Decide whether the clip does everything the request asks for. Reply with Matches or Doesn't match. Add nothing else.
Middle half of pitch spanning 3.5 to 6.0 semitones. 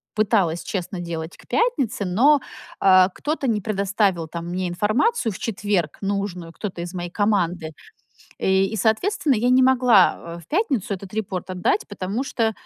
Matches